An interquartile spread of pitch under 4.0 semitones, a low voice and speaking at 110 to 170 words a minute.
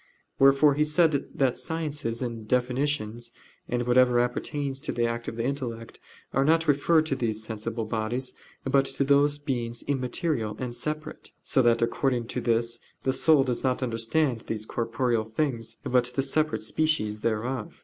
Yes: average, 3.5 semitones; low, 125 Hz; average, 160 wpm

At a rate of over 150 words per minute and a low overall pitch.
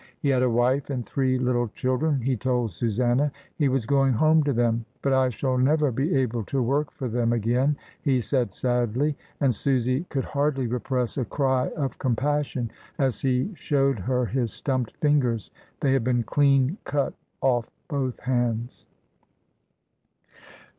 Yes: average, 160 wpm; low, 130 Hz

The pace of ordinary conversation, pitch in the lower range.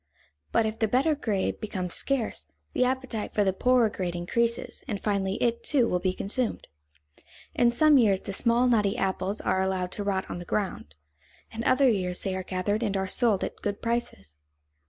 No: average, 190 wpm; high, 205 Hz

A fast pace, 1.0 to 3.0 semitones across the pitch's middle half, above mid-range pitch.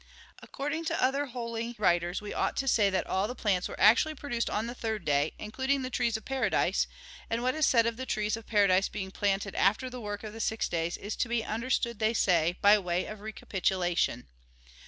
No: fast, 215 wpm; average, 3.7 semitones; high, 220 Hz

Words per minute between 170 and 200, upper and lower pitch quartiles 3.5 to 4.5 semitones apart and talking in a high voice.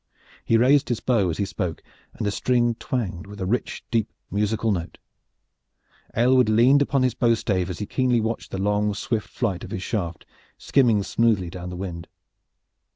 No: average, 180 wpm; average, 3.9 semitones; low, 105 Hz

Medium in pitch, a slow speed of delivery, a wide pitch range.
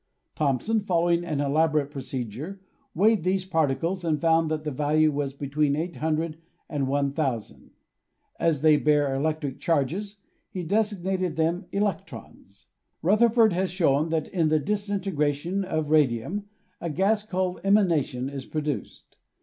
No: medium, 160 Hz; slow, 130 wpm; average, 4.3 semitones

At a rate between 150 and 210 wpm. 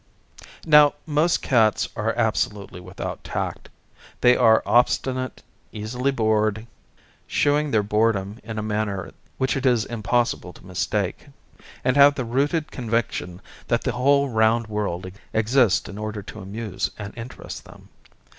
No: average, 140 wpm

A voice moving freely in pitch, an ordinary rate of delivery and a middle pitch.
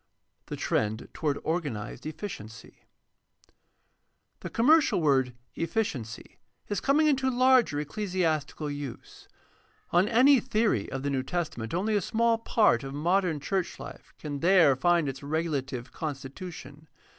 No: wide, 7.0 semitones; slow, 130 wpm; medium, 160 Hz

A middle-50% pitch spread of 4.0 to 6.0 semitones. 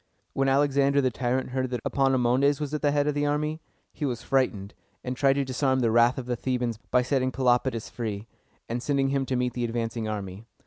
No: narrow, 2.5 semitones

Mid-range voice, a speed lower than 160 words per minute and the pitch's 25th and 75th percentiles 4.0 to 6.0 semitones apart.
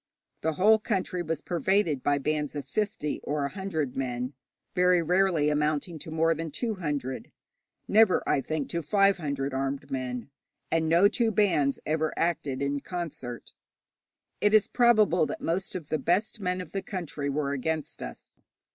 No: medium, 160 Hz; average, 165 wpm; average, 4.8 semitones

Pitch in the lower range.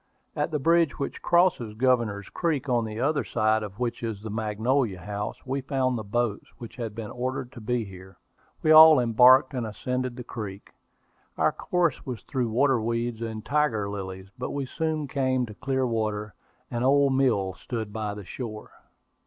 Yes: low, 120 Hz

